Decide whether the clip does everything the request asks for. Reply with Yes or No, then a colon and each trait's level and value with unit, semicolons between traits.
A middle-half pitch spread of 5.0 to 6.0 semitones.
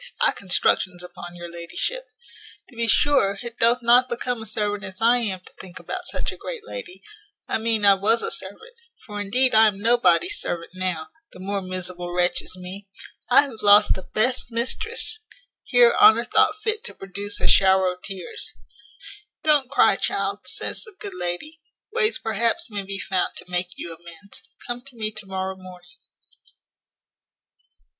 Yes: average, 5.3 semitones